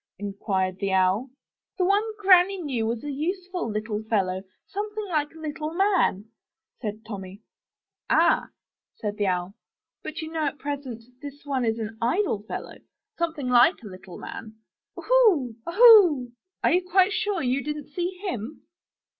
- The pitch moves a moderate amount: No, wide, 8.8 semitones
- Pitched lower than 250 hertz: No, very high, 285 Hz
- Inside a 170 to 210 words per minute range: No, average, 155 wpm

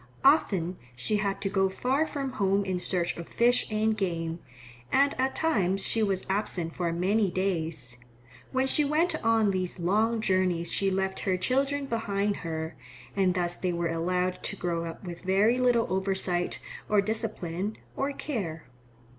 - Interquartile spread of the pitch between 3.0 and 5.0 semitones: Yes, average, 4.1 semitones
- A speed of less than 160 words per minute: No, average, 165 wpm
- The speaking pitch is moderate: No, high, 195 Hz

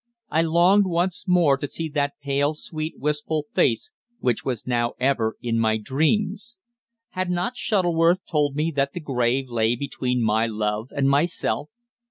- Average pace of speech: Yes, average, 160 wpm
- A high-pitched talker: No, medium, 145 Hz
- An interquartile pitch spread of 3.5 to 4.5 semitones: No, wide, 5.4 semitones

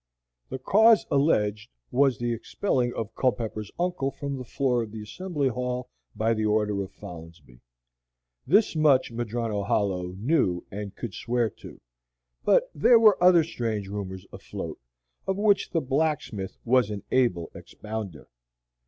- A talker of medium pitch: No, low, 120 Hz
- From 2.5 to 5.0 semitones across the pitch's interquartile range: No, wide, 5.4 semitones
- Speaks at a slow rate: No, average, 145 wpm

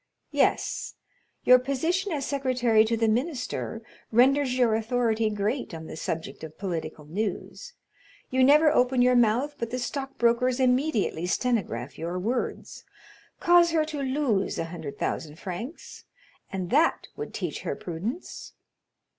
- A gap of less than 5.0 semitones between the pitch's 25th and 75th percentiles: No, wide, 5.5 semitones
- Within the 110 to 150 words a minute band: Yes, average, 140 wpm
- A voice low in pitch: No, high, 245 Hz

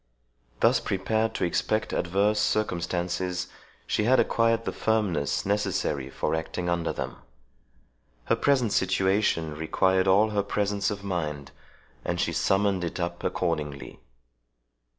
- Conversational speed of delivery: No, slow, 125 wpm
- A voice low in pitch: Yes, very low, 95 Hz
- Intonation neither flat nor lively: Yes, average, 3.4 semitones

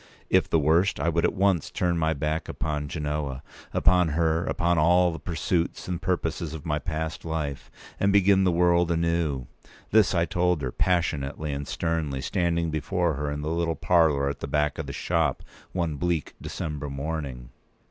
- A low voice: Yes, very low, 80 Hz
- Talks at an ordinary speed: Yes, average, 180 wpm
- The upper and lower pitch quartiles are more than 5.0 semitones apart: No, average, 2.7 semitones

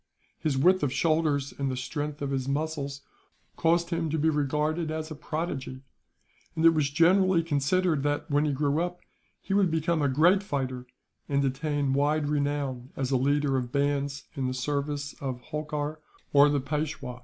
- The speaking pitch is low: No, medium, 145 Hz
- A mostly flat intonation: Yes, narrow, 2.3 semitones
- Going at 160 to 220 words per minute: Yes, average, 180 wpm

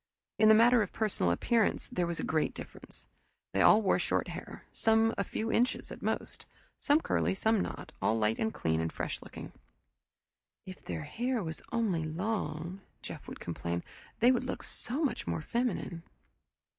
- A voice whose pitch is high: Yes, high, 205 Hz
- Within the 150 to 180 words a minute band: Yes, average, 170 wpm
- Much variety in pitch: Yes, wide, 6.8 semitones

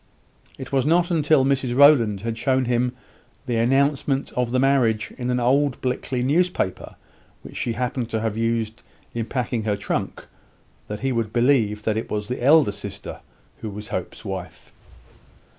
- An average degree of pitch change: Yes, average, 3.3 semitones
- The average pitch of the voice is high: No, low, 120 Hz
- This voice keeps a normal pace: Yes, average, 165 wpm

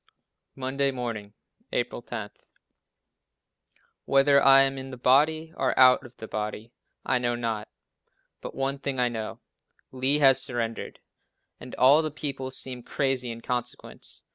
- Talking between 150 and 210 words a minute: No, average, 140 wpm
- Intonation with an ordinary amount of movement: No, narrow, 2.2 semitones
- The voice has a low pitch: Yes, low, 130 Hz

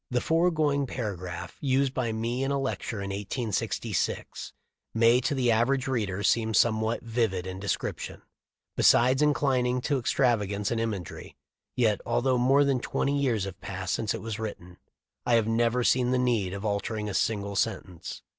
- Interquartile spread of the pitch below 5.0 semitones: Yes, average, 4.0 semitones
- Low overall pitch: Yes, low, 115 Hz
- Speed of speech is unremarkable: Yes, average, 170 wpm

